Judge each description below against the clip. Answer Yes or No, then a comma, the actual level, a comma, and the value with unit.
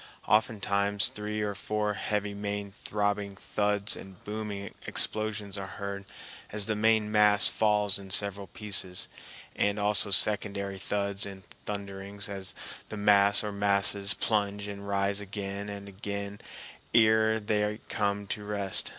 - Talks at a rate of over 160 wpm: No, slow, 135 wpm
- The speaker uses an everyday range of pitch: No, narrow, 0.9 semitones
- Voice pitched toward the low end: Yes, low, 100 Hz